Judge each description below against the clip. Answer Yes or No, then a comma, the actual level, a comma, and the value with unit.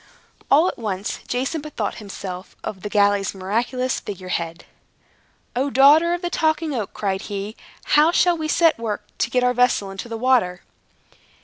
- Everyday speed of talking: Yes, average, 175 wpm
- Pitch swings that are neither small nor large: No, wide, 6.7 semitones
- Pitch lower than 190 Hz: No, high, 235 Hz